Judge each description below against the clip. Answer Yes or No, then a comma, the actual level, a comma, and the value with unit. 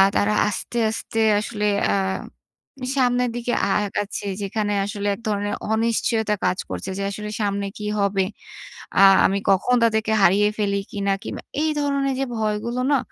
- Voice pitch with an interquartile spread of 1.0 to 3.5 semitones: Yes, narrow, 2.6 semitones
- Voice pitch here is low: No, high, 210 Hz